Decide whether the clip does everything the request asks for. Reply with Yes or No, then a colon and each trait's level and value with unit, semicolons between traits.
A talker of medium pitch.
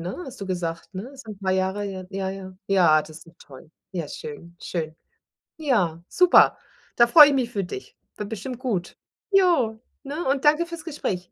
No: high, 200 Hz